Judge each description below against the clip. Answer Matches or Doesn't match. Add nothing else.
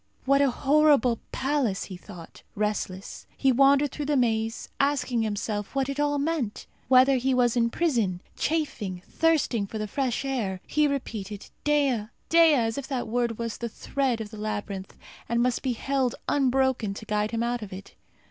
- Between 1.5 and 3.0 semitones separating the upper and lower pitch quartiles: Doesn't match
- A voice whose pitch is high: Matches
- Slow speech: Doesn't match